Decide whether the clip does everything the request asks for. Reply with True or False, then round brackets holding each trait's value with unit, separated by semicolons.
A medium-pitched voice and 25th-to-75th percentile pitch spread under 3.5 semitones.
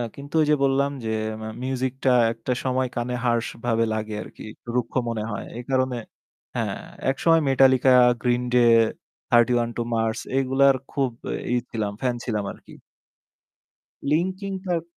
False (125 Hz; 2.5 semitones)